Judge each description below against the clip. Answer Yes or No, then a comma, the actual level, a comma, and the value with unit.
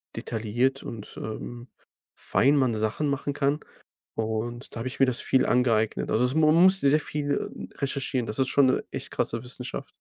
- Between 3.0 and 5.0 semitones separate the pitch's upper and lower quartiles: Yes, average, 3.3 semitones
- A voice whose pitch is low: Yes, low, 130 Hz